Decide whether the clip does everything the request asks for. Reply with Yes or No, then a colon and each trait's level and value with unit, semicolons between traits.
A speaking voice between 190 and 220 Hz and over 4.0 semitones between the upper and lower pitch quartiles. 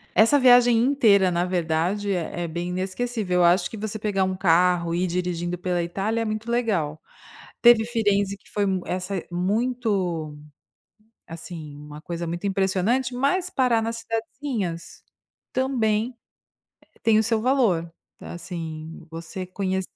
Yes: high, 195 Hz; average, 4.6 semitones